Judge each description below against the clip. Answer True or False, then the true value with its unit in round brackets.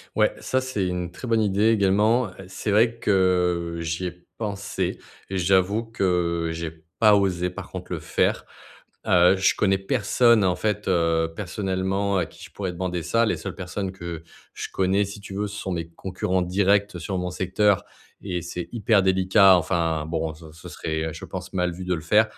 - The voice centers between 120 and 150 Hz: False (95 Hz)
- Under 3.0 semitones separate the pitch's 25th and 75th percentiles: True (2.6 semitones)